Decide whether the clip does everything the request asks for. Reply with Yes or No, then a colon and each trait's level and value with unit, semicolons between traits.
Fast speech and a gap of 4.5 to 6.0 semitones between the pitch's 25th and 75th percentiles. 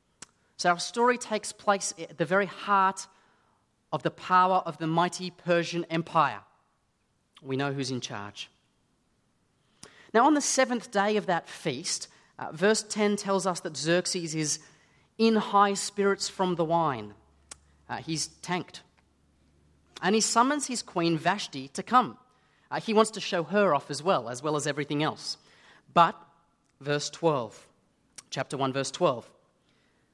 No: average, 150 wpm; average, 5.1 semitones